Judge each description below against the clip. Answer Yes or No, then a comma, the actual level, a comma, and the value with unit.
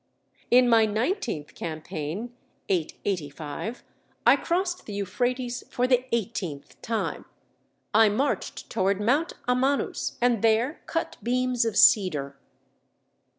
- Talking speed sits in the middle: No, slow, 110 wpm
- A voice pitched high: Yes, high, 225 Hz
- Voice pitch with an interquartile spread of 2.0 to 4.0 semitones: No, average, 4.7 semitones